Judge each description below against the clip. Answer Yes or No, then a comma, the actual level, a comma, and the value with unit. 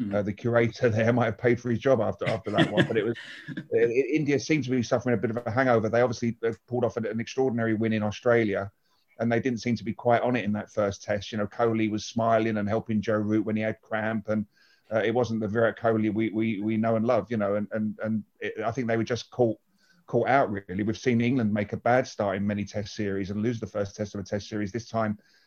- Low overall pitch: Yes, low, 110 Hz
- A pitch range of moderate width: No, narrow, 2.1 semitones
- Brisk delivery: Yes, fast, 270 wpm